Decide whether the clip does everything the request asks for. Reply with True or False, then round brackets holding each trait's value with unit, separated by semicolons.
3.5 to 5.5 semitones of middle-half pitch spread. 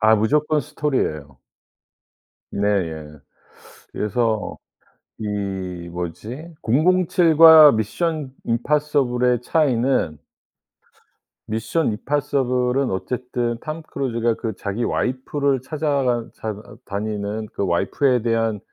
True (5.2 semitones)